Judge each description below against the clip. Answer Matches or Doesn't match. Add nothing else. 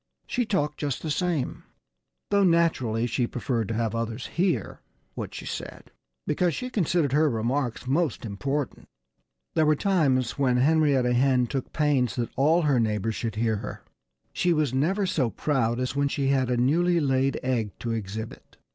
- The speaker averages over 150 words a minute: Matches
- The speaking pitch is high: Doesn't match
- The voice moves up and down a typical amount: Matches